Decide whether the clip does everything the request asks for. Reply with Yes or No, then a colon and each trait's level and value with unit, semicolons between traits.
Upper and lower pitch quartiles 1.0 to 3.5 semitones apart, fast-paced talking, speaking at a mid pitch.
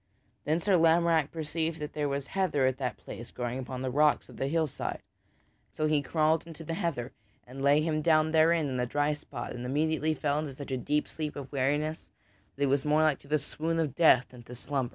Yes: average, 2.7 semitones; fast, 225 wpm; medium, 150 Hz